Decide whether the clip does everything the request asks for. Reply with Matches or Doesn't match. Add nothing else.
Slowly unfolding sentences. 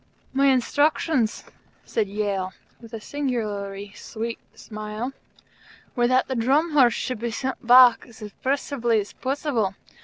Matches